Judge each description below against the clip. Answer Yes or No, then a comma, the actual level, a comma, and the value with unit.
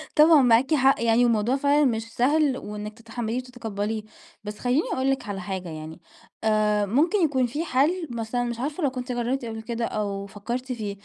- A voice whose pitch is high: Yes, high, 240 Hz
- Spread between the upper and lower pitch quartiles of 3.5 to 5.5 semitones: Yes, average, 3.9 semitones